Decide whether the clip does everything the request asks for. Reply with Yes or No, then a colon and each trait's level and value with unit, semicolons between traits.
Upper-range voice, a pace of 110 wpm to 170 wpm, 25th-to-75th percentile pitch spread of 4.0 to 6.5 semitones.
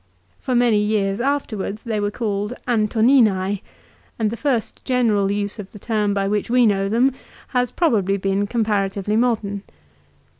No: high, 210 Hz; average, 155 wpm; average, 3.0 semitones